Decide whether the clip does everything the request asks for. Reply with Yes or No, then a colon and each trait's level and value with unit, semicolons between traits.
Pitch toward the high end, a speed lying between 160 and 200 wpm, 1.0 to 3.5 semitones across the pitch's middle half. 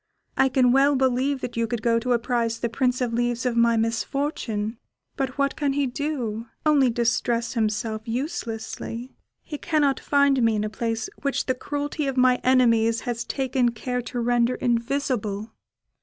Yes: high, 245 Hz; average, 170 wpm; average, 2.7 semitones